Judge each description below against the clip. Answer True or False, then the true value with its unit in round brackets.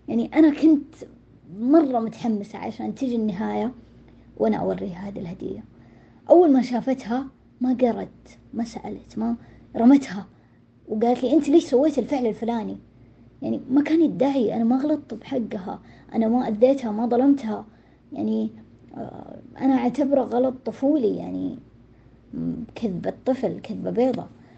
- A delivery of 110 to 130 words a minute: True (120 wpm)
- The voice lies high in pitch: True (235 Hz)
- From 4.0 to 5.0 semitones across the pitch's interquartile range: True (4.4 semitones)